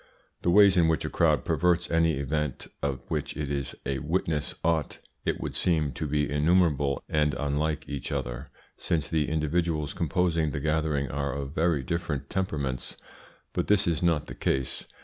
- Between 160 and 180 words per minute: Yes, average, 170 wpm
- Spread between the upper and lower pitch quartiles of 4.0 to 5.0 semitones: No, average, 2.9 semitones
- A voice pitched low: Yes, very low, 75 Hz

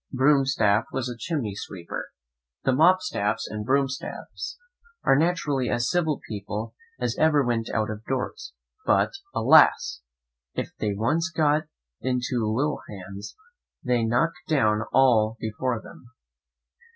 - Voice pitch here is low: Yes, low, 125 Hz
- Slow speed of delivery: Yes, slow, 125 wpm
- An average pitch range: Yes, average, 5.0 semitones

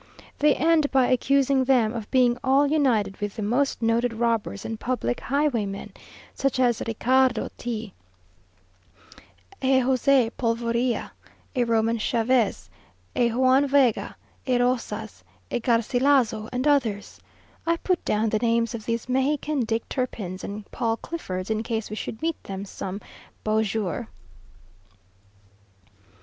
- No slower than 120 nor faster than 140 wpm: Yes, slow, 135 wpm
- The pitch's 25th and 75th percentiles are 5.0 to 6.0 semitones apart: No, average, 3.2 semitones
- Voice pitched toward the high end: Yes, high, 235 Hz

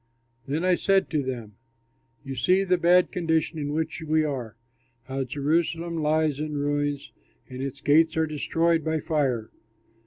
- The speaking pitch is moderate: Yes, medium, 155 Hz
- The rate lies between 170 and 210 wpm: No, average, 155 wpm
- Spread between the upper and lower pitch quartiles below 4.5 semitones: Yes, average, 3.0 semitones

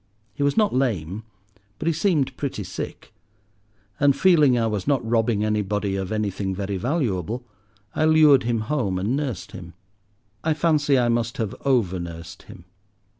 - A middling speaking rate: Yes, average, 160 wpm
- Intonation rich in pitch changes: Yes, wide, 6.4 semitones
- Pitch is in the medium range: No, low, 115 Hz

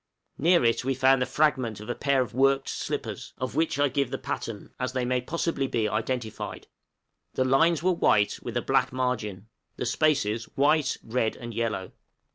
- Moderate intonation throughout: Yes, average, 3.2 semitones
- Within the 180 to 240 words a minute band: Yes, average, 185 wpm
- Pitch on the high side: No, low, 130 Hz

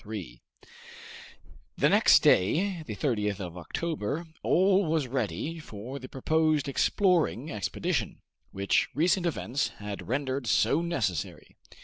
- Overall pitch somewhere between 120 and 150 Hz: Yes, low, 135 Hz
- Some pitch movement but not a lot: No, wide, 7.7 semitones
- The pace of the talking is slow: Yes, slow, 120 wpm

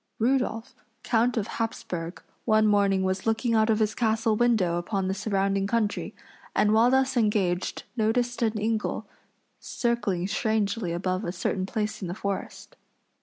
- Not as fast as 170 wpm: Yes, average, 150 wpm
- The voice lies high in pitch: Yes, high, 215 Hz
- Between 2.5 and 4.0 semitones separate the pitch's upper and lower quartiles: Yes, average, 2.8 semitones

